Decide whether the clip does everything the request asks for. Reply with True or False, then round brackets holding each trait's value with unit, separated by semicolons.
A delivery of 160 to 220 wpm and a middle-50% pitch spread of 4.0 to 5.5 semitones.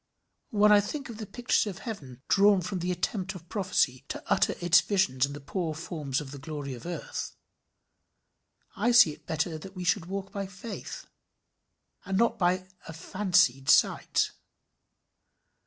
True (165 wpm; 4.5 semitones)